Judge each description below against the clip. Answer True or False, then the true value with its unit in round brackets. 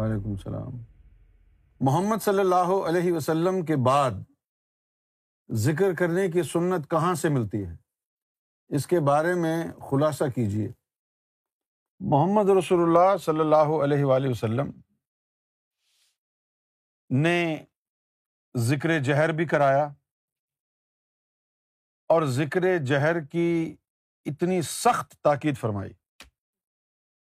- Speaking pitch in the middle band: True (155 Hz)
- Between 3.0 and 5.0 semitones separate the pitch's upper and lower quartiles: False (5.5 semitones)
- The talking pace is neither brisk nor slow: False (95 wpm)